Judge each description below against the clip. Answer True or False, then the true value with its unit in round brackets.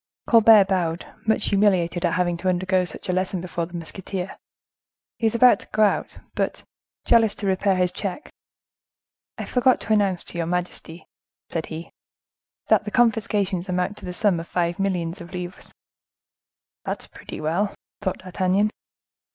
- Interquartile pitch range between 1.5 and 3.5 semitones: True (2.8 semitones)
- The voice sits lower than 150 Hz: False (185 Hz)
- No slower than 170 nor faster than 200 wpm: False (160 wpm)